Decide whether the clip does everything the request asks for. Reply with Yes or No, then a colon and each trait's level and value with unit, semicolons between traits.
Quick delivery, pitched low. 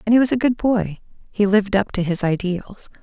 No: fast, 240 wpm; high, 205 Hz